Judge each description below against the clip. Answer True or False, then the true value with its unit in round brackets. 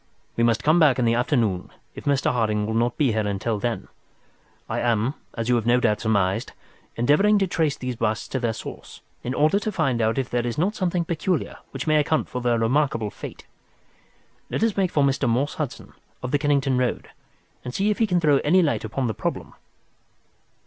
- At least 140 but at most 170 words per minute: False (205 wpm)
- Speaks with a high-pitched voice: False (125 Hz)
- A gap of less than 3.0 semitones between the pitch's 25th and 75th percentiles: False (5.0 semitones)